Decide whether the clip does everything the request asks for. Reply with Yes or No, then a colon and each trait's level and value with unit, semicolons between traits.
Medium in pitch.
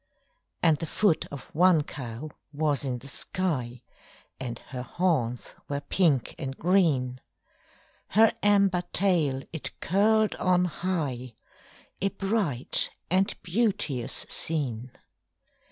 Yes: medium, 155 Hz